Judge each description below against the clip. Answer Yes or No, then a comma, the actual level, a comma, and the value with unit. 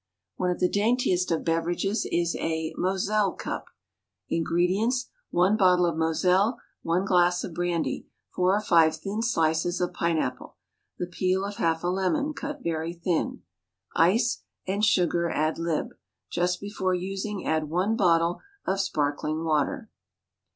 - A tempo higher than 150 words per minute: No, average, 145 wpm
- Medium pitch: Yes, medium, 180 Hz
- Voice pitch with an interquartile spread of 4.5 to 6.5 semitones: No, average, 3.0 semitones